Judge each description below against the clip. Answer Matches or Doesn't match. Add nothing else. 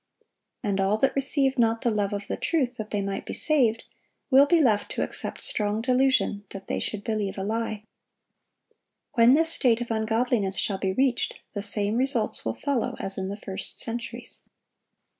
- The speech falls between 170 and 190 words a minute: Matches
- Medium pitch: Doesn't match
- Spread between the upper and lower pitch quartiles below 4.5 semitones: Matches